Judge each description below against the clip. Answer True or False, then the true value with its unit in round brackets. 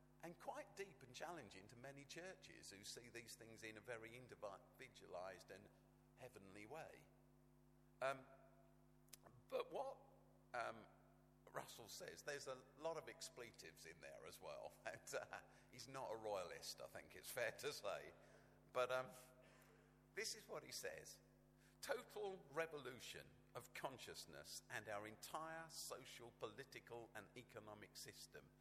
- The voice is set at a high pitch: False (130 Hz)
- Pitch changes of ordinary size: False (6.2 semitones)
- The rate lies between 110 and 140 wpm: True (135 wpm)